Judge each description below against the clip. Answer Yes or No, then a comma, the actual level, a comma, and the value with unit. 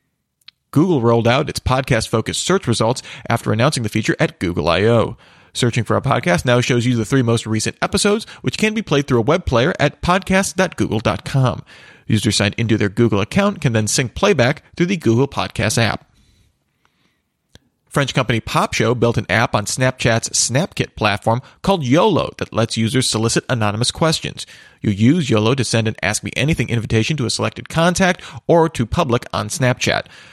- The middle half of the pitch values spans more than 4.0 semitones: Yes, average, 4.5 semitones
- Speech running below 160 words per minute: No, average, 180 wpm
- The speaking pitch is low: Yes, low, 120 Hz